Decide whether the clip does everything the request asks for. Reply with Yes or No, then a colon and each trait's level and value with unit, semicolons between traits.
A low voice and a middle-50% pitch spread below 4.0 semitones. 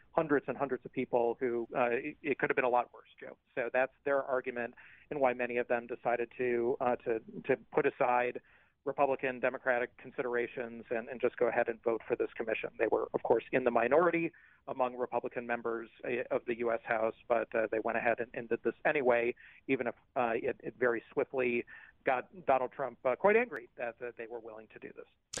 Yes: low, 125 Hz; average, 2.8 semitones